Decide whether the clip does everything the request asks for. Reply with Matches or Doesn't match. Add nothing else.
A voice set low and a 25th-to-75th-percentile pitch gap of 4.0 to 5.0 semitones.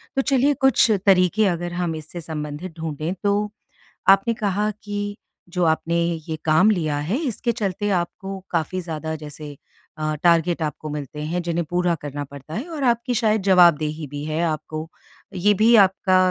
Doesn't match